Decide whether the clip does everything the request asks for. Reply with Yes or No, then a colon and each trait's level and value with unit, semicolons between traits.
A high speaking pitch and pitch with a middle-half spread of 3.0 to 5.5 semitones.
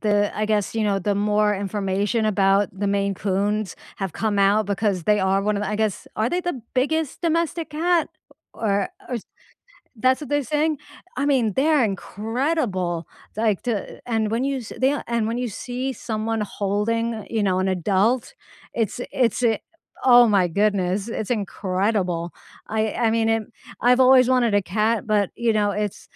Yes: high, 215 Hz; average, 3.4 semitones